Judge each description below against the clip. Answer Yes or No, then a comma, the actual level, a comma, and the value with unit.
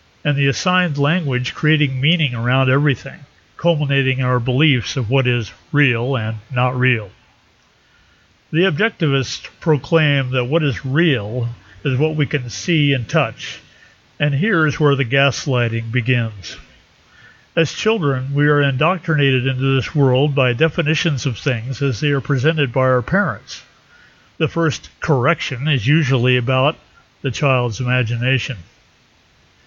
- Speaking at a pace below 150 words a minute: Yes, average, 140 wpm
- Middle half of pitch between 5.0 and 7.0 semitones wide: No, average, 3.1 semitones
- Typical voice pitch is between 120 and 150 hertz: Yes, low, 135 Hz